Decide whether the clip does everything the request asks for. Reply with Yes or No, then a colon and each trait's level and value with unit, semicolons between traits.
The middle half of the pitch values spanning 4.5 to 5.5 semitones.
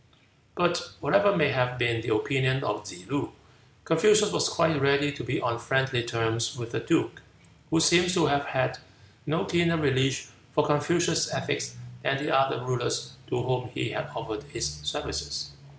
Yes: average, 5.0 semitones